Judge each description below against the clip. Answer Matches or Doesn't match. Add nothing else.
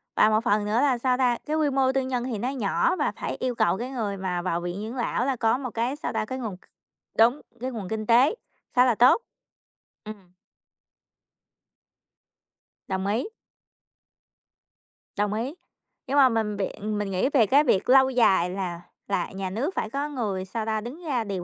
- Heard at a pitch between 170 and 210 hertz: Doesn't match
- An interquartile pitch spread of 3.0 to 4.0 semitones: Doesn't match